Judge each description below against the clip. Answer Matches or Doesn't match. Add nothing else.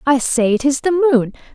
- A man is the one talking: Doesn't match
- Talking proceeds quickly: Matches